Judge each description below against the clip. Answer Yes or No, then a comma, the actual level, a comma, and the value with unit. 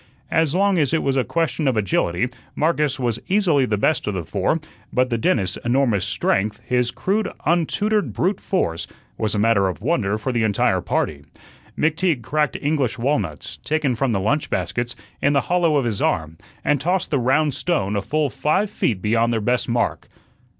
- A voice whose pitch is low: Yes, low, 130 Hz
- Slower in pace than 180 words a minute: No, average, 185 wpm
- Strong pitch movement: Yes, wide, 6.3 semitones